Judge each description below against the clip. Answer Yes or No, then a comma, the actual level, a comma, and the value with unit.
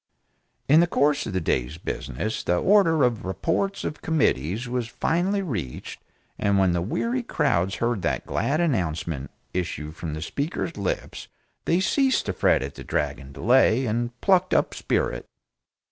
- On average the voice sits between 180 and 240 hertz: No, low, 115 Hz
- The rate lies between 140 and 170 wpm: Yes, average, 160 wpm